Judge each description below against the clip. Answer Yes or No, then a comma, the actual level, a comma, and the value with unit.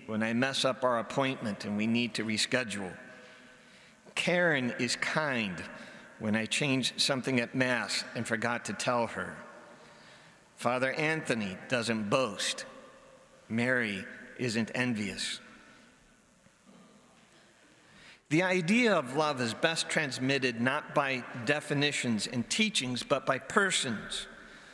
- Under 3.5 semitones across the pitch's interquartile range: No, average, 3.9 semitones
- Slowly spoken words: Yes, slow, 115 wpm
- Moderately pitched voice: No, low, 125 Hz